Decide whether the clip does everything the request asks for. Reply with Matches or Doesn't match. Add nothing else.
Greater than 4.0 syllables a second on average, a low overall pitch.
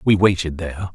Matches